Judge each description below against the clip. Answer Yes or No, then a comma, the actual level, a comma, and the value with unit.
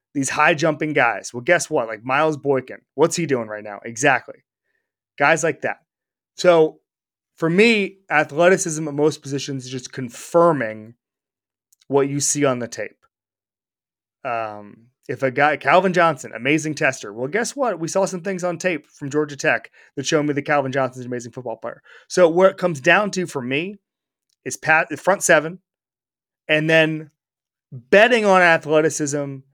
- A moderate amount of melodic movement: Yes, average, 4.4 semitones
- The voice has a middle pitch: Yes, medium, 150 Hz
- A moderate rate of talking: Yes, average, 170 wpm